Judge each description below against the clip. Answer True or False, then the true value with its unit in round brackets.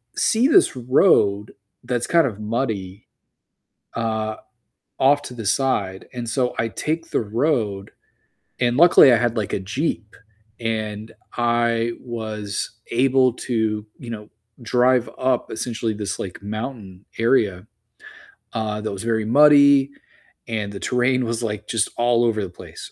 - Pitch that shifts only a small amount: False (3.0 semitones)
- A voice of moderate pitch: False (115 Hz)